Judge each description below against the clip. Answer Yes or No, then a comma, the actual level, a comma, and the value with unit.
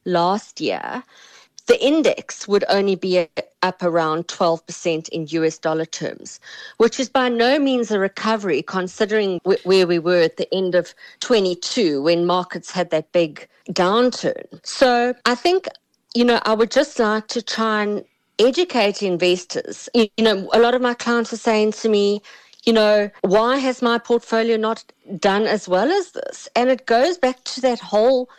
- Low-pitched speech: No, high, 220 Hz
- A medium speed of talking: Yes, average, 175 wpm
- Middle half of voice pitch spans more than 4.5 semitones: Yes, average, 5.0 semitones